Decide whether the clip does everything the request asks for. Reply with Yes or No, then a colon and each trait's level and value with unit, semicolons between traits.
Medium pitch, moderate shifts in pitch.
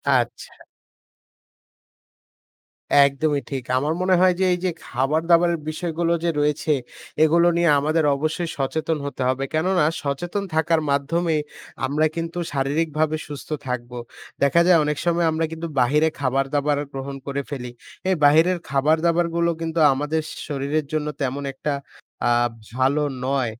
Yes: medium, 155 Hz; average, 3.1 semitones